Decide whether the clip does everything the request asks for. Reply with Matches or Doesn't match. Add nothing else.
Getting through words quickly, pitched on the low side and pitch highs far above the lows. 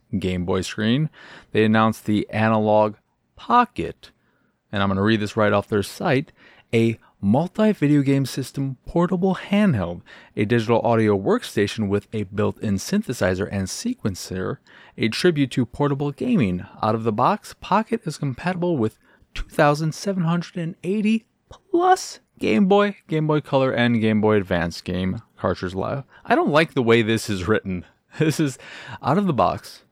Doesn't match